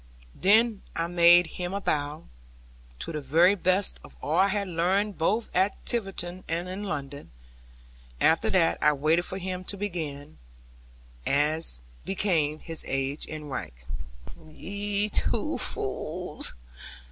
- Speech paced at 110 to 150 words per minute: Yes, average, 140 wpm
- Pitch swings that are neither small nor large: Yes, average, 4.1 semitones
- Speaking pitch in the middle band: Yes, medium, 175 Hz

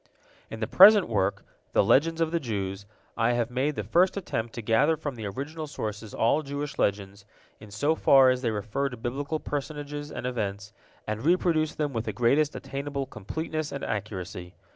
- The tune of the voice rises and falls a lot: Yes, wide, 5.7 semitones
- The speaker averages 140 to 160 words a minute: No, average, 185 wpm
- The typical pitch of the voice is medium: No, low, 130 Hz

